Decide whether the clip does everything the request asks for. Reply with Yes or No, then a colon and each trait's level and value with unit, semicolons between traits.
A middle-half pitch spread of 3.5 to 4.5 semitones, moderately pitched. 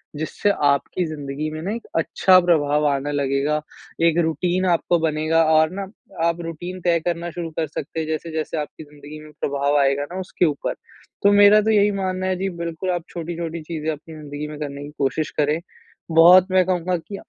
No: average, 3.0 semitones; medium, 160 Hz